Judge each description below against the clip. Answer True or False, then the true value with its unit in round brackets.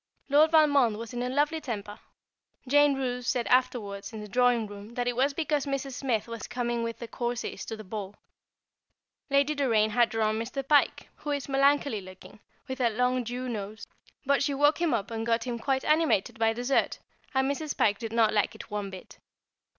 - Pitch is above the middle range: True (245 Hz)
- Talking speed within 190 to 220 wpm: True (195 wpm)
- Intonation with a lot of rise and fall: False (3.8 semitones)